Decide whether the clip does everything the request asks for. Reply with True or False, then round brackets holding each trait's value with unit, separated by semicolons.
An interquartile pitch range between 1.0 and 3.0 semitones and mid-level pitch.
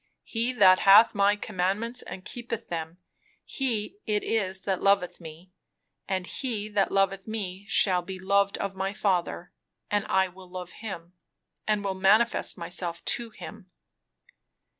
False (2.4 semitones; 195 Hz)